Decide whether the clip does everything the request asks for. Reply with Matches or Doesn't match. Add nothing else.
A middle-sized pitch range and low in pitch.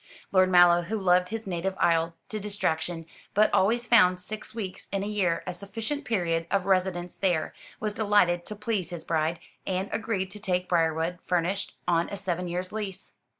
Doesn't match